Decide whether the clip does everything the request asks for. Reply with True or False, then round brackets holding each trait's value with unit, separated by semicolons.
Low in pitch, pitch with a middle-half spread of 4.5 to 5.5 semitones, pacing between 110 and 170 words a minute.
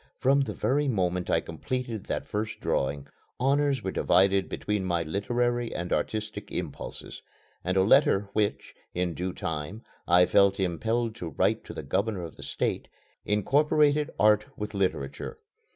True (105 Hz; 5.0 semitones; 150 wpm)